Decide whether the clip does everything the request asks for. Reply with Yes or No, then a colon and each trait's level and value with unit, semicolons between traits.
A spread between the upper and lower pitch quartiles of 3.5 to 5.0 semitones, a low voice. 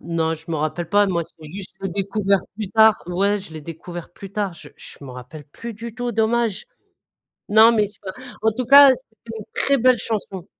No: average, 4.6 semitones; high, 200 Hz